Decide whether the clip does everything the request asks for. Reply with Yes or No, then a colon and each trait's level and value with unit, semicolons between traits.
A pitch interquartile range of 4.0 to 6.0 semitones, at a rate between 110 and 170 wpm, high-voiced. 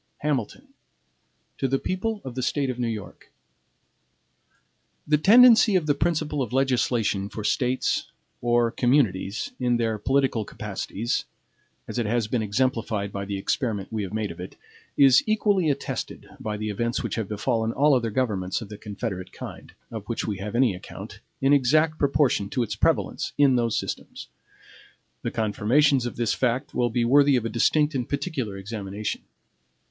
No: average, 4.7 semitones; average, 165 wpm; low, 120 Hz